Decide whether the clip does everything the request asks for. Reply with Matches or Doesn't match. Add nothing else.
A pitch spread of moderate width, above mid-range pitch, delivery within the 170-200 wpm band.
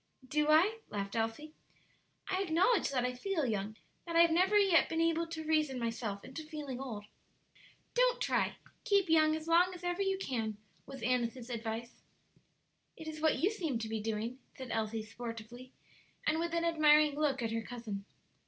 Doesn't match